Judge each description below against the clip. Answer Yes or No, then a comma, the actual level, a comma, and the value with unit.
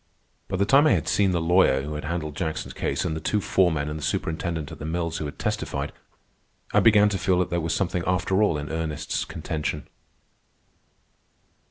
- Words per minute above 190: Yes, average, 200 wpm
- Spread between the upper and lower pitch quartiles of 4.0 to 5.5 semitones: No, average, 3.4 semitones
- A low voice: Yes, very low, 85 Hz